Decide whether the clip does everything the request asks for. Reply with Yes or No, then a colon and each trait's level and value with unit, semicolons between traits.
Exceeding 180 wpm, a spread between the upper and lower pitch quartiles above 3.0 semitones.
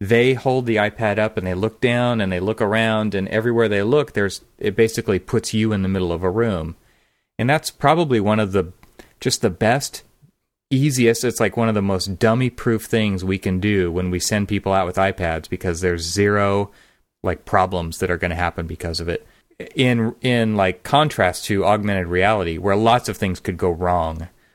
Yes: fast, 205 wpm; average, 3.7 semitones